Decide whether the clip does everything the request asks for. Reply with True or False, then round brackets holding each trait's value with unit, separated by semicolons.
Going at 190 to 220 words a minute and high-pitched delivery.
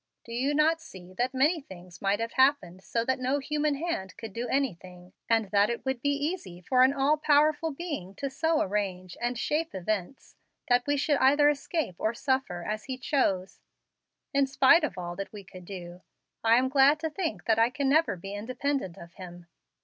True (200 wpm; 250 Hz)